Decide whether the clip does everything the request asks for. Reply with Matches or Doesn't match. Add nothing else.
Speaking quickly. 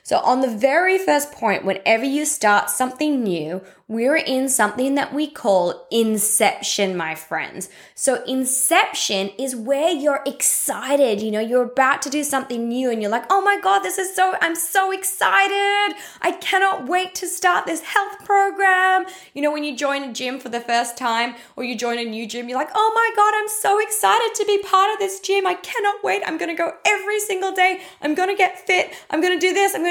Matches